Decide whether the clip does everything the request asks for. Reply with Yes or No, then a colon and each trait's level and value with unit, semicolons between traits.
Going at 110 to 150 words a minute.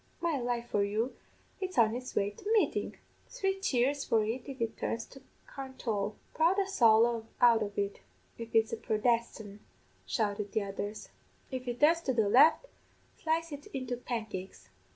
No: average, 170 wpm